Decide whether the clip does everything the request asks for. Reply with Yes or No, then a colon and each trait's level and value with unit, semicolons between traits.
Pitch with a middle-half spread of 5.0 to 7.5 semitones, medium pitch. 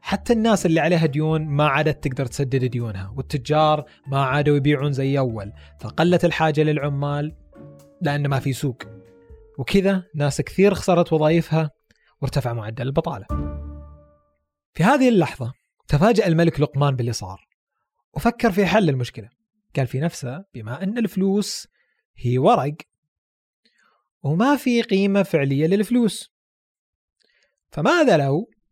Yes: wide, 5.4 semitones; medium, 150 Hz